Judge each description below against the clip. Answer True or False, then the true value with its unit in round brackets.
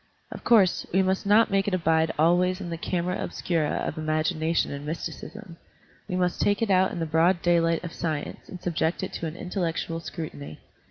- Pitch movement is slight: True (2.3 semitones)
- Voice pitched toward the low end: False (170 Hz)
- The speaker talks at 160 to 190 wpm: False (205 wpm)